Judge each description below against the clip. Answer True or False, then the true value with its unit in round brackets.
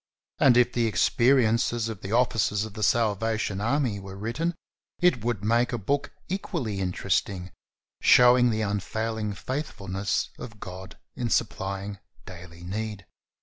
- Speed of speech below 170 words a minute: True (140 wpm)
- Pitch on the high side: False (110 Hz)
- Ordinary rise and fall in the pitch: True (3.4 semitones)